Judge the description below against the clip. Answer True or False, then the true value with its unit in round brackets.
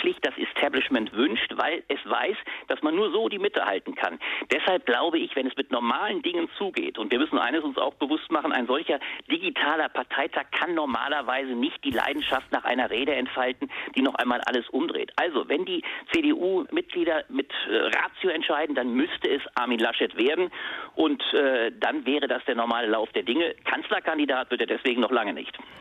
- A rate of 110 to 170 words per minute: False (185 wpm)